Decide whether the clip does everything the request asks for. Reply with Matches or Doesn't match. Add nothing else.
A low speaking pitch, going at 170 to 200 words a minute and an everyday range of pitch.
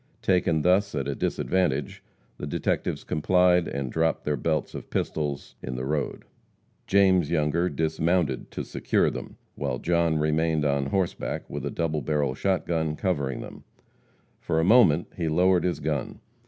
Doesn't match